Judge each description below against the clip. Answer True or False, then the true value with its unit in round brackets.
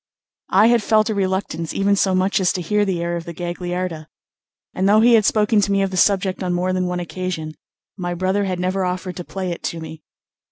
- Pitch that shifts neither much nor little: False (2.0 semitones)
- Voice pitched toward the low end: False (185 Hz)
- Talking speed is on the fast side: True (235 wpm)